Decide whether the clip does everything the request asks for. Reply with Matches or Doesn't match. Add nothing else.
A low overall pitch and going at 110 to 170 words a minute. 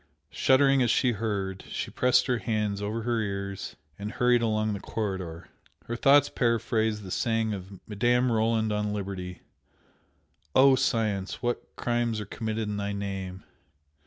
Matches